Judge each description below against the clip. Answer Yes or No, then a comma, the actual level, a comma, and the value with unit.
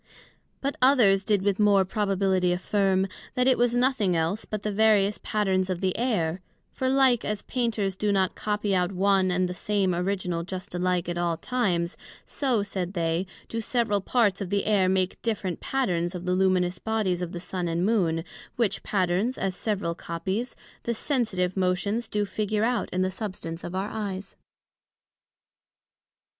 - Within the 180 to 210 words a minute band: No, average, 170 wpm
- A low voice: No, high, 195 Hz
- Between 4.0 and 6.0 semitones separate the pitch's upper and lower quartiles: No, average, 3.0 semitones